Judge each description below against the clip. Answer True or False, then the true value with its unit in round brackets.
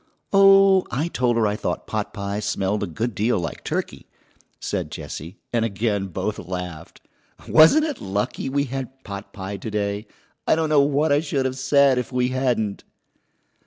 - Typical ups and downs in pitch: False (5.7 semitones)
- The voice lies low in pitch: True (115 Hz)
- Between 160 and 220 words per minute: True (165 wpm)